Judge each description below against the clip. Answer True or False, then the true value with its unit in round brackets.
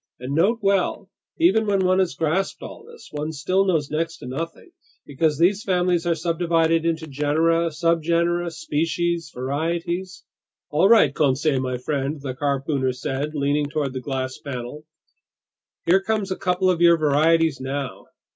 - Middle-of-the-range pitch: True (160 Hz)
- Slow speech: False (155 wpm)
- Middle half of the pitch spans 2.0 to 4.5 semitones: True (3.4 semitones)